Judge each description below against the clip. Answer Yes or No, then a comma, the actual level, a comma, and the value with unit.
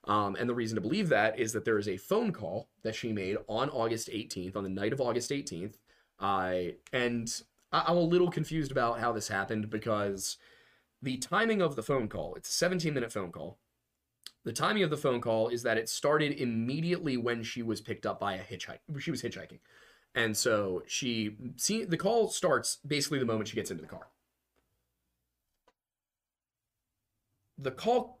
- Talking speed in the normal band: Yes, average, 185 wpm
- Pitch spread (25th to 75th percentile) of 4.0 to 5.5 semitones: Yes, average, 5.1 semitones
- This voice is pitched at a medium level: No, low, 115 Hz